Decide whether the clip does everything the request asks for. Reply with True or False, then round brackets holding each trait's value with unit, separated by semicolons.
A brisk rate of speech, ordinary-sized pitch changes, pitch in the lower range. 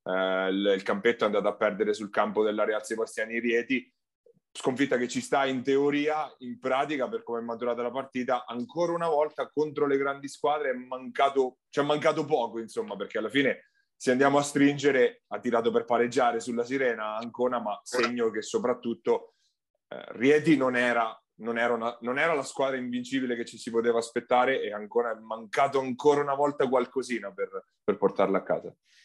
True (190 wpm; 3.5 semitones; 125 Hz)